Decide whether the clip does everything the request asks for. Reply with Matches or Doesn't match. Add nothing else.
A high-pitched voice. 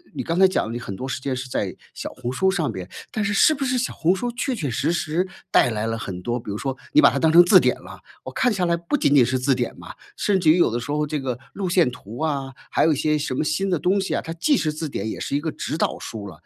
Doesn't match